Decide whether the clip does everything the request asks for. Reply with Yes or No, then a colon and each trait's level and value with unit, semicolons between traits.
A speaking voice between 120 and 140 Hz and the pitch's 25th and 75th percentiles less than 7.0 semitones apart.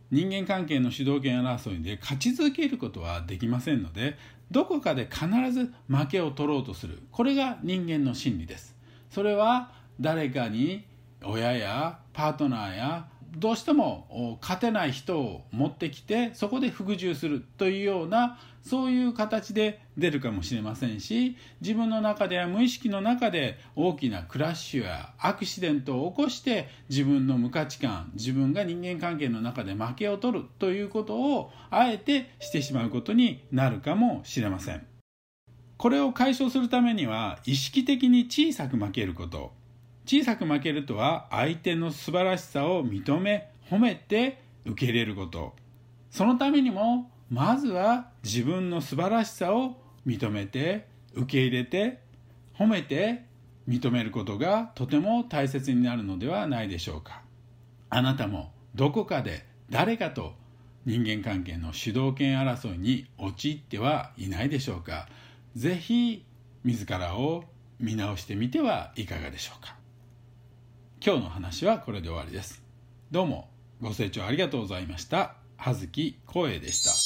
No: low, 135 Hz; wide, 8.6 semitones